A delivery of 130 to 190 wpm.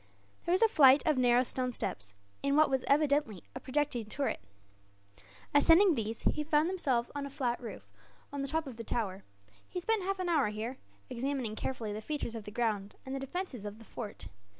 No: average, 200 wpm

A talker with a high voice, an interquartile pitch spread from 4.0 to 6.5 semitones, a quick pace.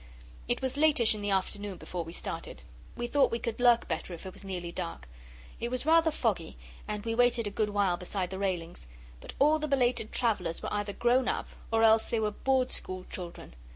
Yes: high, 215 Hz; average, 4.7 semitones; fast, 215 wpm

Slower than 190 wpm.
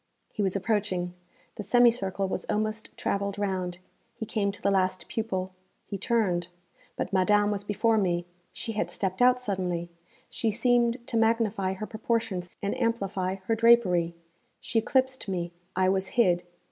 Yes: average, 155 wpm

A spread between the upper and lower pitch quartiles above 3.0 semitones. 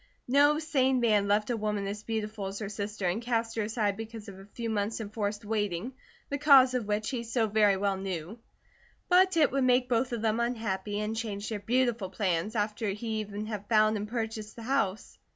No: narrow, 2.5 semitones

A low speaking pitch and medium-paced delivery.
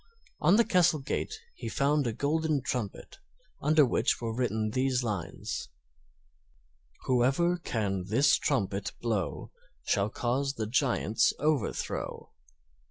No: low, 130 Hz; slow, 115 wpm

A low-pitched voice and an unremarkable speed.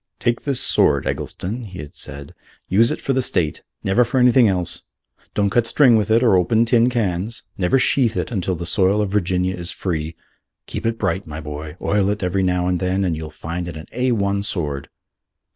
No: very low, 95 Hz; fast, 210 wpm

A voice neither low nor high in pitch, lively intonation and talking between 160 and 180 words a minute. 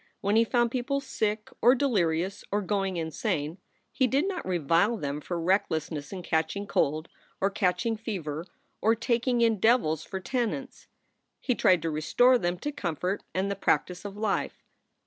No: high, 200 Hz; wide, 5.8 semitones; average, 165 wpm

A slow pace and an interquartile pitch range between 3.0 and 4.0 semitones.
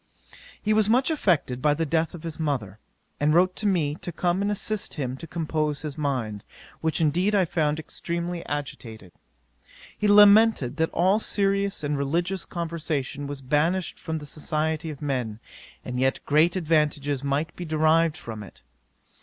No: average, 165 wpm; average, 3.5 semitones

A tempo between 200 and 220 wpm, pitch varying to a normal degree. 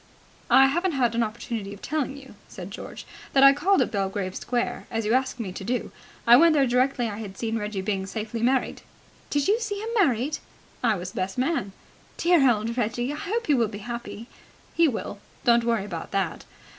Yes: fast, 205 wpm; average, 4.6 semitones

